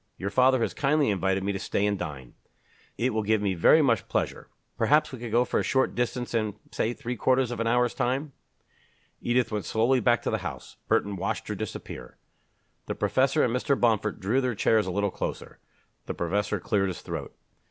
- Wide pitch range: No, average, 4.1 semitones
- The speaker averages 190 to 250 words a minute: Yes, fast, 205 wpm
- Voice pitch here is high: No, low, 115 Hz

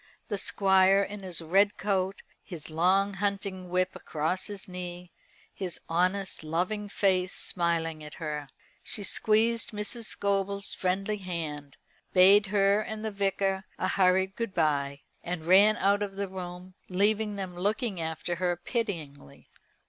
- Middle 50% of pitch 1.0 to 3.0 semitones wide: Yes, narrow, 2.4 semitones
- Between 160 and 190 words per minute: No, average, 140 wpm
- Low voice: No, high, 190 Hz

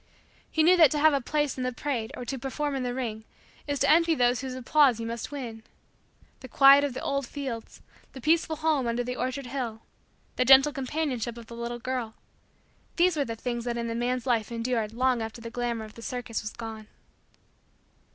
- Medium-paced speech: No, fast, 210 wpm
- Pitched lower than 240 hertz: No, very high, 250 Hz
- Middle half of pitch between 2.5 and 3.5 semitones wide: Yes, average, 3.1 semitones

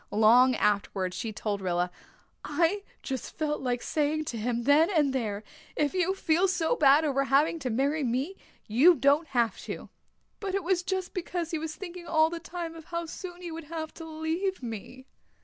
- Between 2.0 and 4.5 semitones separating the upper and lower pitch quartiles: No, average, 5.1 semitones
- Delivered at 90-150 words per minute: No, average, 190 wpm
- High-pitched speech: Yes, very high, 310 Hz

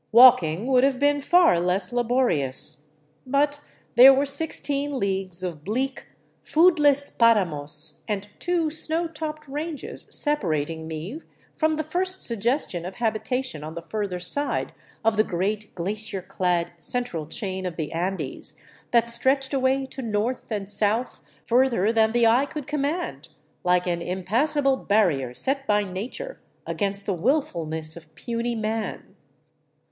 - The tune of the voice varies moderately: No, wide, 7.2 semitones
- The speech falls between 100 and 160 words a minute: Yes, average, 140 wpm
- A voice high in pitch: Yes, high, 225 Hz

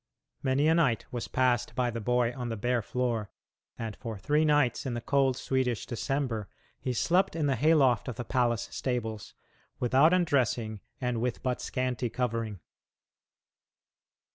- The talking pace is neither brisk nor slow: Yes, average, 160 wpm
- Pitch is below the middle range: Yes, low, 125 Hz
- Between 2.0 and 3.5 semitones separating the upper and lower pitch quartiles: Yes, narrow, 2.6 semitones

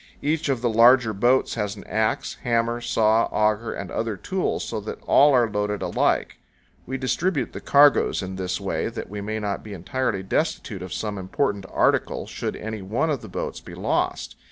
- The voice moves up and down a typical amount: Yes, average, 3.6 semitones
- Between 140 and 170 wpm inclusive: No, average, 190 wpm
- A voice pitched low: Yes, low, 110 Hz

